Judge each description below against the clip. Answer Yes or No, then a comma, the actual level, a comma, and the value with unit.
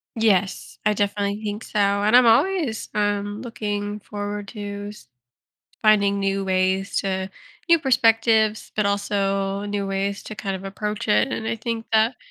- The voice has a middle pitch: No, high, 205 Hz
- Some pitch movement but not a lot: No, narrow, 1.6 semitones